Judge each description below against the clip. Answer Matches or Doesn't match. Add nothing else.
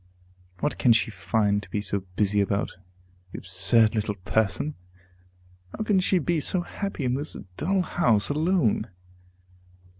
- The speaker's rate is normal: Matches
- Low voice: Matches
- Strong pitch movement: Matches